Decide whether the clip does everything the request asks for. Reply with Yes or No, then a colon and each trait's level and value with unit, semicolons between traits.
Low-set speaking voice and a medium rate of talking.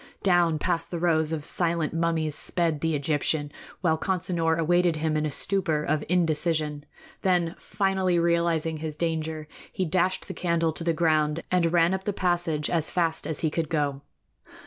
No: medium, 165 Hz; average, 170 wpm